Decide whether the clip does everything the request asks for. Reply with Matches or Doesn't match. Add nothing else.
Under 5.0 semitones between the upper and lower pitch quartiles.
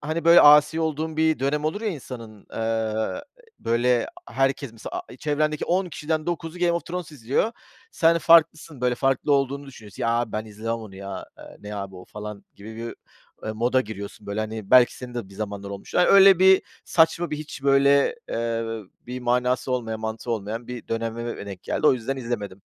Doesn't match